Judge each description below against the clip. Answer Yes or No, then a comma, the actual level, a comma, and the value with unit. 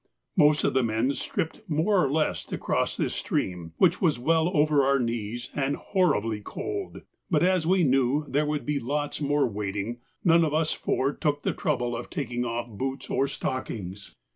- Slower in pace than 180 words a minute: No, average, 185 wpm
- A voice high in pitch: No, medium, 140 Hz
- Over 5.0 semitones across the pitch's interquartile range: No, average, 4.6 semitones